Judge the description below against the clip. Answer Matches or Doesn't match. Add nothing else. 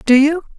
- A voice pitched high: Matches